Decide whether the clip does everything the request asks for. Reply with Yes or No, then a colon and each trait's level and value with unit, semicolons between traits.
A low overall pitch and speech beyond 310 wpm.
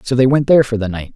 Yes: low, 120 Hz; fast, 365 wpm